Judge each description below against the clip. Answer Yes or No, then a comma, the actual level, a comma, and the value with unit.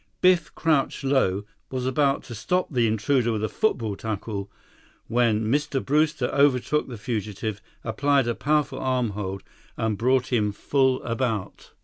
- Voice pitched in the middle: No, low, 125 Hz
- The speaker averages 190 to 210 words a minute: No, average, 145 wpm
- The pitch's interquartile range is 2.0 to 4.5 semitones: Yes, average, 4.2 semitones